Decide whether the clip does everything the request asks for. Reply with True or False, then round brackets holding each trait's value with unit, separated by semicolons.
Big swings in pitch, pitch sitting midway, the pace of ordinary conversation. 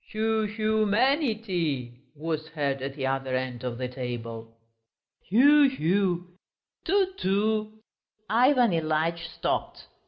False (8.3 semitones; 175 Hz; 120 wpm)